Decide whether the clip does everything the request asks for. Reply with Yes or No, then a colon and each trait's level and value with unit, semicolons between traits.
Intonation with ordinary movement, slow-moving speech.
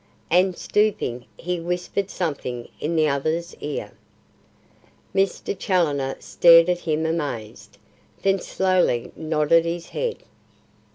Yes: average, 3.3 semitones; slow, 110 wpm